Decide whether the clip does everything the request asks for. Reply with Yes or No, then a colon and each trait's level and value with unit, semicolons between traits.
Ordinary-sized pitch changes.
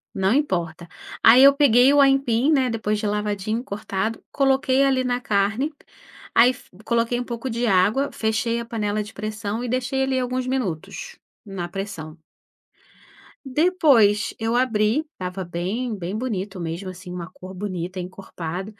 Yes: average, 4.8 semitones